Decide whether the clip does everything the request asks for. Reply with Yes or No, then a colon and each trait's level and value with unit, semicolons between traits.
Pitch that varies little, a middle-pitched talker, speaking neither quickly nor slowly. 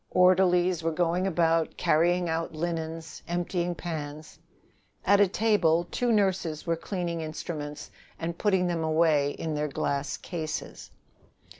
No: narrow, 2.2 semitones; medium, 170 Hz; slow, 130 wpm